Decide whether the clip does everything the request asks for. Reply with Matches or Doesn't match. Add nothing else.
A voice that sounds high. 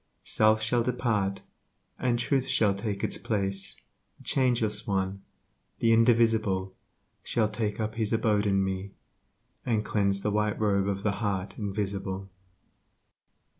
Doesn't match